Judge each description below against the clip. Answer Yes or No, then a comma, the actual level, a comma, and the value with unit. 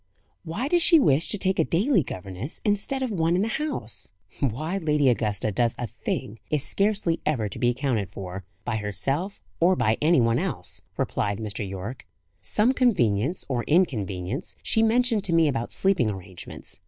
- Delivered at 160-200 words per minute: Yes, average, 175 wpm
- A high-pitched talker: No, medium, 140 Hz